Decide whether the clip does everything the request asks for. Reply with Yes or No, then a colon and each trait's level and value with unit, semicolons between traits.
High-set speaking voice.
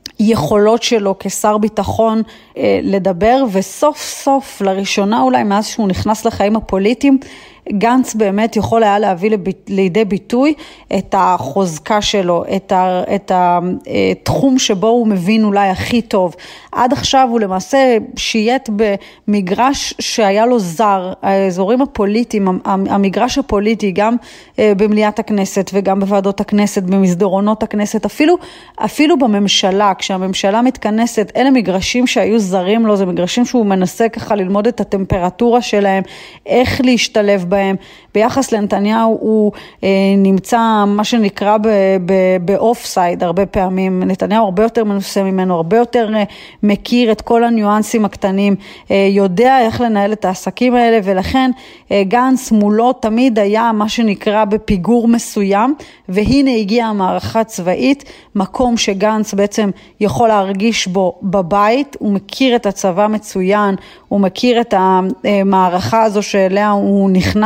Yes: high, 210 Hz